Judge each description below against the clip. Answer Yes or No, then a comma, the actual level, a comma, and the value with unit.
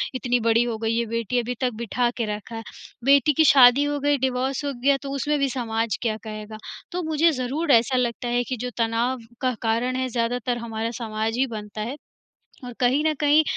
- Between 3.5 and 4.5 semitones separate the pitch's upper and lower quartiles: No, average, 2.9 semitones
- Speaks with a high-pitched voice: Yes, high, 245 Hz